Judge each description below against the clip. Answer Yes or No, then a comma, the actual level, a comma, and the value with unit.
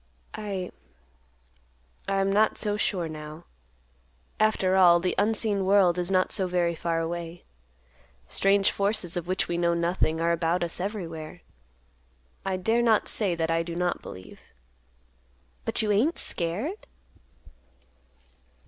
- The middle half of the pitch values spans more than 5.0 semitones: No, average, 2.9 semitones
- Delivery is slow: Yes, slow, 130 wpm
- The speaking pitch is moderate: Yes, medium, 180 Hz